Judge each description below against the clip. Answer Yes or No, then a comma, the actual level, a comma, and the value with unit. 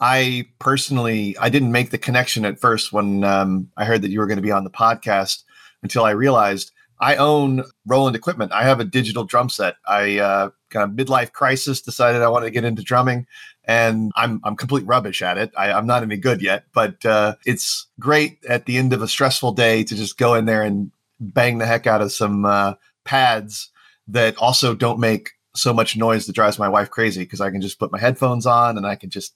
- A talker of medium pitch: No, low, 115 Hz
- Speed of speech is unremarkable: No, fast, 225 wpm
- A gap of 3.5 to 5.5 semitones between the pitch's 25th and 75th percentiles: No, average, 3.1 semitones